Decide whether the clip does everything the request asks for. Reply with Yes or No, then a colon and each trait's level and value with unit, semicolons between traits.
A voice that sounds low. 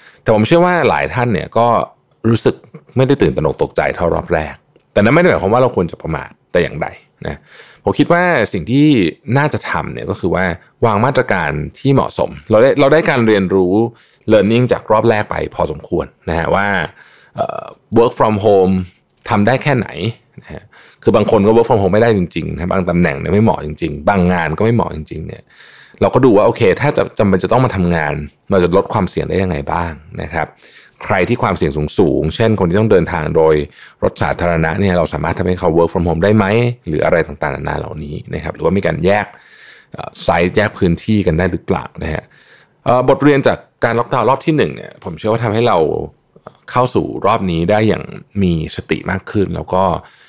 Yes: low, 100 Hz